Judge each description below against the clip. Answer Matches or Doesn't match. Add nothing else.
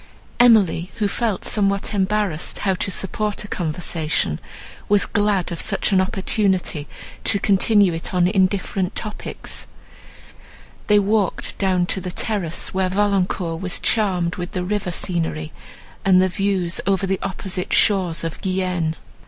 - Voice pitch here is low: Doesn't match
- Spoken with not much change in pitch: Matches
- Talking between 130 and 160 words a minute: Matches